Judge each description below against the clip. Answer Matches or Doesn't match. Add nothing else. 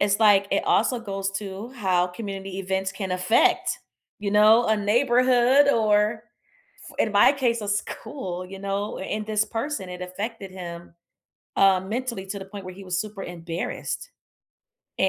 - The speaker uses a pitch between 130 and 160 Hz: Doesn't match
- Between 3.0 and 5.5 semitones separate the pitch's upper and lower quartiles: Doesn't match